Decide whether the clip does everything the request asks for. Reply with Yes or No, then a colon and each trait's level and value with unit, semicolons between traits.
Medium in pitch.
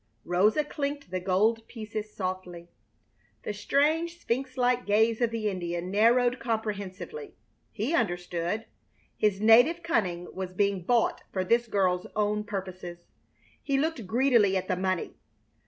No: high, 215 Hz